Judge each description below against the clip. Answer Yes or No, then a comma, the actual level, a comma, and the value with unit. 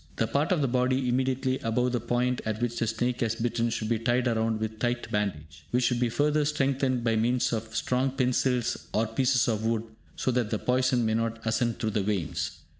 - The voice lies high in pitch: No, low, 120 Hz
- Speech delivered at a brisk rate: Yes, fast, 215 wpm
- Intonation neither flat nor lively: No, narrow, 2.2 semitones